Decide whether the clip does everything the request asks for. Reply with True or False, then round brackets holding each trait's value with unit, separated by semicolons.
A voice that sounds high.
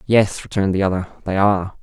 False (100 Hz)